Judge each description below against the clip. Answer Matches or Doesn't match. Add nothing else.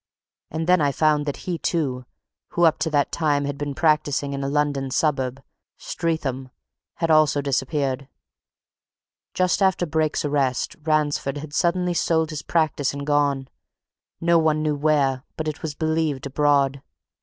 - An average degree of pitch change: Doesn't match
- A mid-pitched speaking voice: Matches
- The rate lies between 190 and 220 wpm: Doesn't match